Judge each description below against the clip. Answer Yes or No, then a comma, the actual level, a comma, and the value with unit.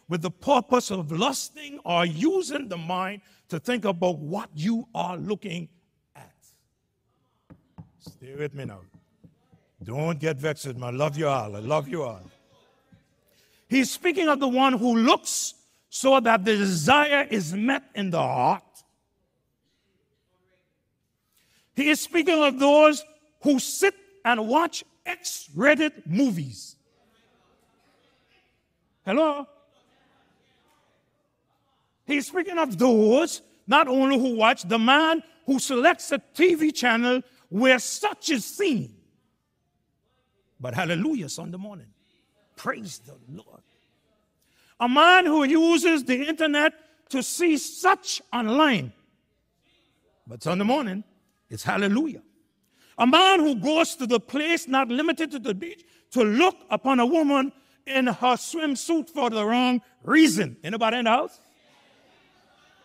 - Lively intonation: Yes, wide, 7.5 semitones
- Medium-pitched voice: No, very high, 255 Hz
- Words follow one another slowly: Yes, slow, 125 wpm